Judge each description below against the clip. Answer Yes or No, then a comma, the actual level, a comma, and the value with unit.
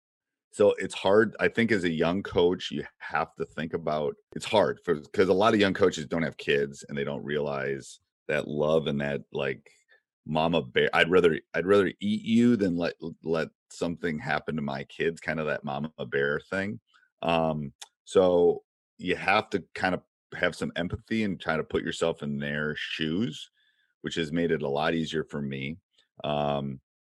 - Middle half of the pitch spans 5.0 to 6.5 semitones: Yes, average, 5.3 semitones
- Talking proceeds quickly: No, average, 185 wpm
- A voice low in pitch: Yes, very low, 80 Hz